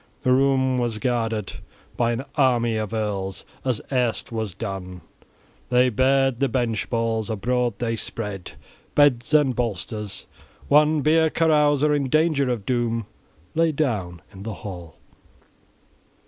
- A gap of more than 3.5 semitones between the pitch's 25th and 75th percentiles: Yes, average, 3.9 semitones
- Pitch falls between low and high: No, low, 120 Hz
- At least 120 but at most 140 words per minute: Yes, slow, 135 wpm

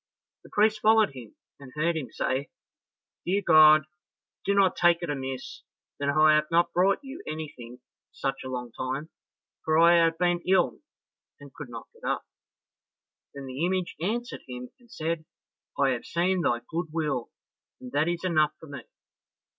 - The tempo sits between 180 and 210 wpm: No, average, 170 wpm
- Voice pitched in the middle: Yes, medium, 160 Hz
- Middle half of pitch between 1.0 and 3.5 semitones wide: No, average, 4.5 semitones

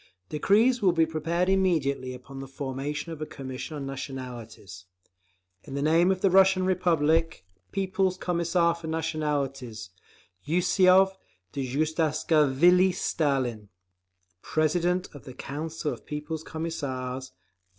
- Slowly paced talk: Yes, slow, 120 wpm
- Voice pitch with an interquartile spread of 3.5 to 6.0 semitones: Yes, average, 4.4 semitones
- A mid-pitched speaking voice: Yes, medium, 155 Hz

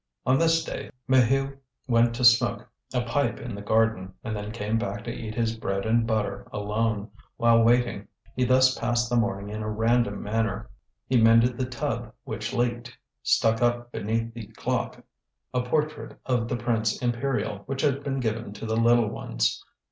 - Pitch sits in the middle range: No, low, 115 Hz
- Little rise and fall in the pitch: Yes, narrow, 1.9 semitones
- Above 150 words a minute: Yes, average, 180 wpm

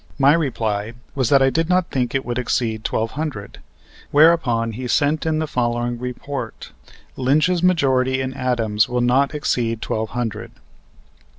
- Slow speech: No, average, 155 wpm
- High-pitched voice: No, low, 130 Hz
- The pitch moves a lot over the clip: No, average, 3.7 semitones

